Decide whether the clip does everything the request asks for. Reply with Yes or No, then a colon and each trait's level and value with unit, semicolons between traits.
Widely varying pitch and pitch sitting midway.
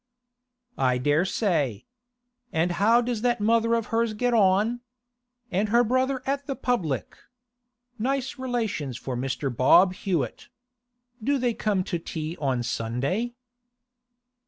No: wide, 8.6 semitones; high, 205 Hz